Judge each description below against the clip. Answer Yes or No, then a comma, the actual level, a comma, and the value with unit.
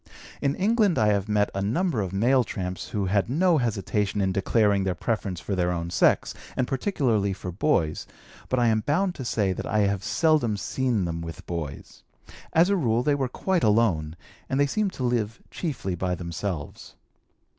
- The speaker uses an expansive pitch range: Yes, wide, 6.1 semitones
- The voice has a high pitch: No, low, 105 Hz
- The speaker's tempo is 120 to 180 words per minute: No, average, 190 wpm